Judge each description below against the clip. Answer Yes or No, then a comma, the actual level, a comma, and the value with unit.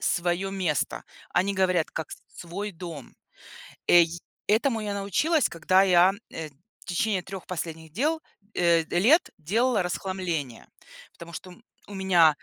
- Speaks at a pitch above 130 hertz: Yes, medium, 185 Hz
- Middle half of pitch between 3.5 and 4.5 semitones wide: No, average, 3.0 semitones